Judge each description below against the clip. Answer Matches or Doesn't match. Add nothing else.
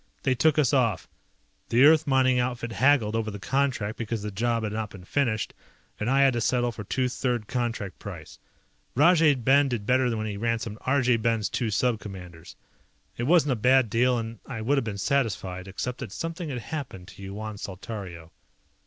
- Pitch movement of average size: Matches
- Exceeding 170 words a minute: Matches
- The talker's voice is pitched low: Matches